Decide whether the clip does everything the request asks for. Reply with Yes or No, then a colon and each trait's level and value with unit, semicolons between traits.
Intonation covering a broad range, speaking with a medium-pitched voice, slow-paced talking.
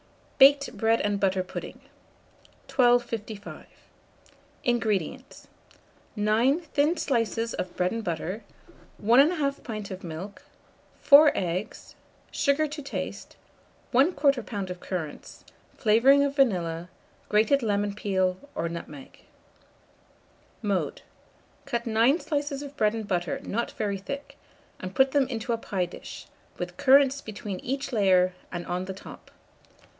No: wide, 6.2 semitones; high, 220 Hz; slow, 125 wpm